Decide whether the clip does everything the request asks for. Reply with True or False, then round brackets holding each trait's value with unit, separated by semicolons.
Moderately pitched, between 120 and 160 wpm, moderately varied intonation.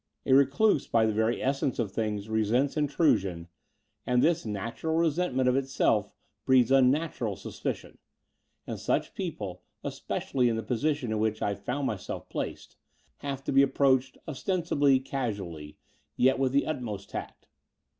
False (130 Hz; 150 wpm; 4.1 semitones)